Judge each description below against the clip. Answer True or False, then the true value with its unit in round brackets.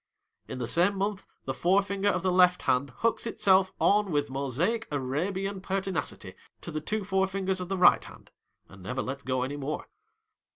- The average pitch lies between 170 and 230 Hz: True (185 Hz)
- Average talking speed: True (175 wpm)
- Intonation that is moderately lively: False (5.7 semitones)